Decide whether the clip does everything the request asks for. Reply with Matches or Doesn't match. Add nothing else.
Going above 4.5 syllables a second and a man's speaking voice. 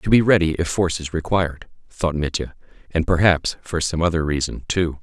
Matches